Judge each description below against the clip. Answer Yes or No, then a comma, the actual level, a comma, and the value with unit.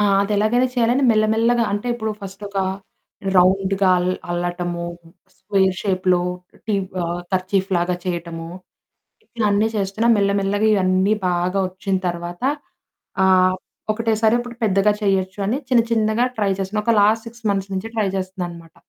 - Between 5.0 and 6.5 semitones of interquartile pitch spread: No, average, 2.8 semitones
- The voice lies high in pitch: Yes, high, 195 Hz